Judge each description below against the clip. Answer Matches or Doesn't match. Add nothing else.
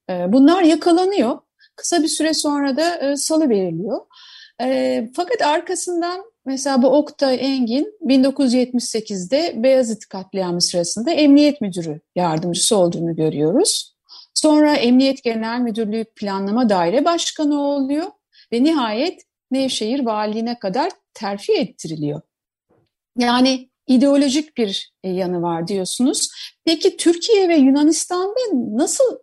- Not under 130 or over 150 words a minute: Doesn't match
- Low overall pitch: Doesn't match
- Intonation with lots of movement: Matches